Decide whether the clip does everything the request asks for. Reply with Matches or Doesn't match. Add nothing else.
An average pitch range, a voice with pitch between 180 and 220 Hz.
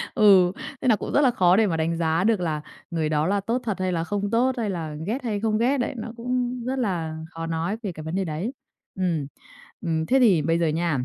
Doesn't match